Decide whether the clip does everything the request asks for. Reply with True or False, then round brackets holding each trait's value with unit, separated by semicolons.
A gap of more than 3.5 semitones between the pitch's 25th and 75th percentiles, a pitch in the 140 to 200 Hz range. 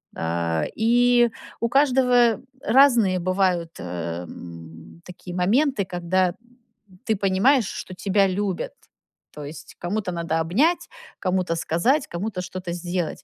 True (5.3 semitones; 185 Hz)